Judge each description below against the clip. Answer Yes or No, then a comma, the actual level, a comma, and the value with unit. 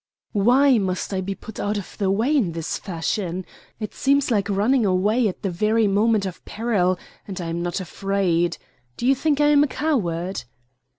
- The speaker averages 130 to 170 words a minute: No, average, 190 wpm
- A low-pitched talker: No, high, 200 Hz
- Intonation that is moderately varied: Yes, average, 4.4 semitones